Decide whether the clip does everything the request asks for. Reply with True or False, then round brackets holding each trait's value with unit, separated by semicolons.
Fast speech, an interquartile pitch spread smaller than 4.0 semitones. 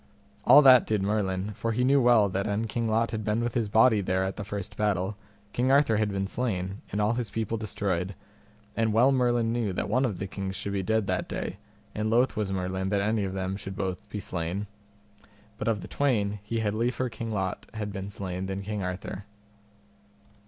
True (215 wpm; 2.9 semitones)